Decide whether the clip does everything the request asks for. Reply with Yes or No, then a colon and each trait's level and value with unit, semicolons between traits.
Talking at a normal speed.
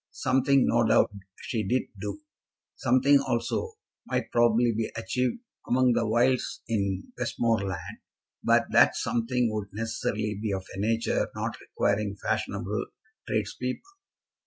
No: slow, 125 wpm